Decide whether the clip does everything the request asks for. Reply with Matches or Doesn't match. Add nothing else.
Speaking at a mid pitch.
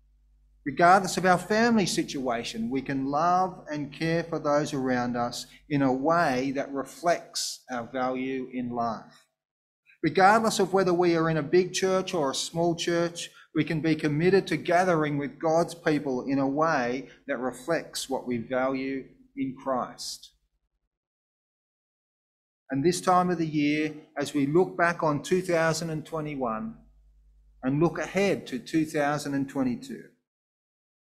Matches